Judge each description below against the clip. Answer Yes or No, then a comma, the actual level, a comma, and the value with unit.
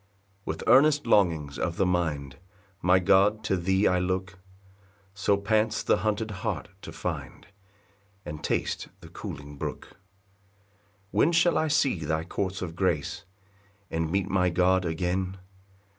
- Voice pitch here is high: No, very low, 95 Hz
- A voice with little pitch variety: No, average, 3.2 semitones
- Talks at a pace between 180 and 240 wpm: No, average, 145 wpm